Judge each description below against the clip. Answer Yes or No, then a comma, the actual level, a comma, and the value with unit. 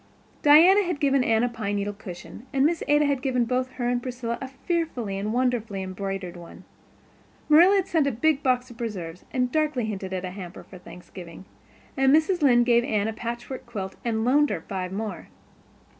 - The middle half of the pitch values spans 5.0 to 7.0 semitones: Yes, wide, 5.6 semitones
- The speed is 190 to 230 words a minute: Yes, average, 195 wpm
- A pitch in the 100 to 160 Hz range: No, high, 240 Hz